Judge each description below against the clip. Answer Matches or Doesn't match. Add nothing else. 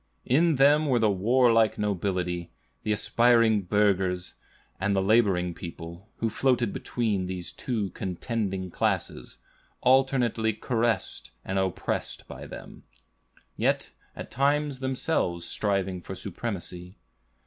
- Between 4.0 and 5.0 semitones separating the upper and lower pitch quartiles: Matches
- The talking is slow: Matches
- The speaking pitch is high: Doesn't match